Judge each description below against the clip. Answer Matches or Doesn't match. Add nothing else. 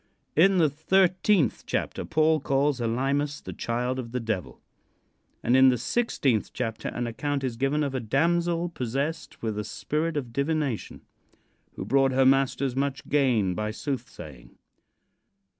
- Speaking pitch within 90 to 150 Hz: Matches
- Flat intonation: Doesn't match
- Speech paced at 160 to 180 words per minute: Doesn't match